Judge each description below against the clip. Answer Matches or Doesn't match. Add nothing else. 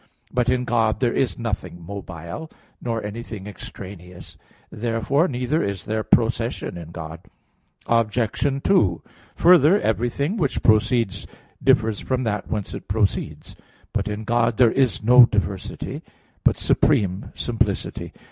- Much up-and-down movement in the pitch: Doesn't match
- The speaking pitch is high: Doesn't match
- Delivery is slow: Matches